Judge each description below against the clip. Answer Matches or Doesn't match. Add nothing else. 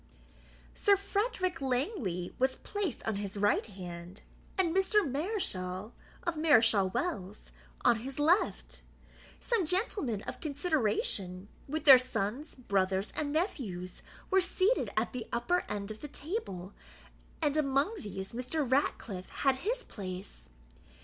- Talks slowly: Matches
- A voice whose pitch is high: Matches